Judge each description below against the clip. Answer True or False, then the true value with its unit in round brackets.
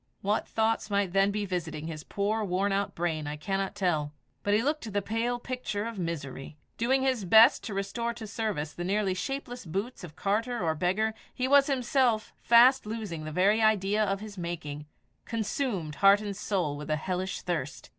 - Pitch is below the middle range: False (200 Hz)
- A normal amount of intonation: True (4.3 semitones)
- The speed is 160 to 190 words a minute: True (185 wpm)